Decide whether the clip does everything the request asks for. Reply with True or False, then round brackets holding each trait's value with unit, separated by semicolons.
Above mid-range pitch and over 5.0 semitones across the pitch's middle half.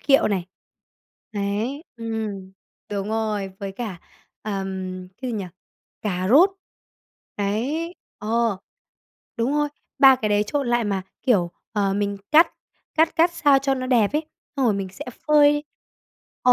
True (220 Hz; 5.4 semitones)